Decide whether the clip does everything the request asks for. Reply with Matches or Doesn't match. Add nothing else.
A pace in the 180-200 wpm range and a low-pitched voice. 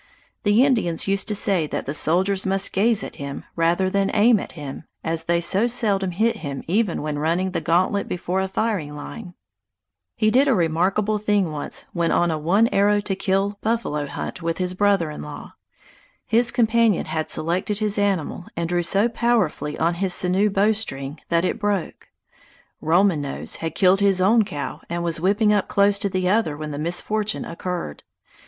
Doesn't match